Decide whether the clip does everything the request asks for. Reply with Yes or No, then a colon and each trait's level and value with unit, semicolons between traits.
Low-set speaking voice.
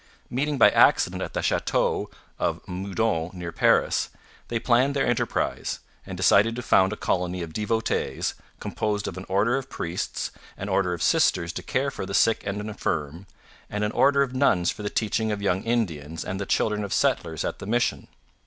Yes: low, 105 Hz